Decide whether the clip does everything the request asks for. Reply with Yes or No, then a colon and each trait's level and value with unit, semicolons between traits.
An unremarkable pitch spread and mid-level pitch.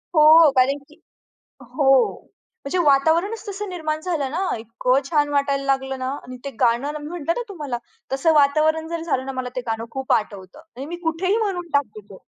No: average, 3.8 semitones; very high, 290 Hz